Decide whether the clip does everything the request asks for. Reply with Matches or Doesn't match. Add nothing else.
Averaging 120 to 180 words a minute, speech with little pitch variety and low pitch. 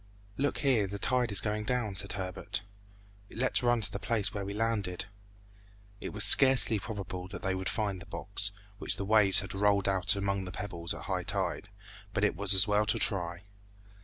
Doesn't match